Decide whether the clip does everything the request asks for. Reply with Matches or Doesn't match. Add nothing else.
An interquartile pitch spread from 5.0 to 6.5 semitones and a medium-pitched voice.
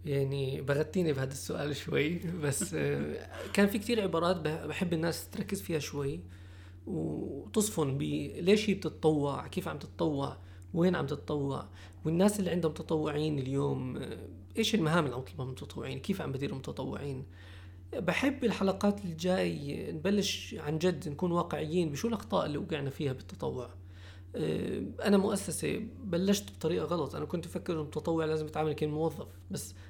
Matches